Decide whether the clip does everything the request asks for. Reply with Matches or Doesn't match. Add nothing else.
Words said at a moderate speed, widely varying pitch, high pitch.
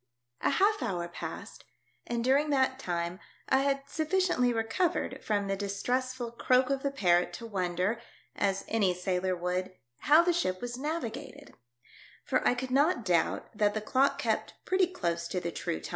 Matches